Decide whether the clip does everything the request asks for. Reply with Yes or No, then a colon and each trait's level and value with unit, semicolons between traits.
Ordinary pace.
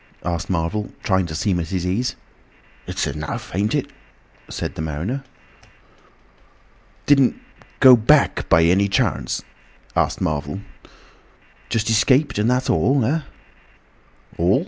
No: slow, 125 wpm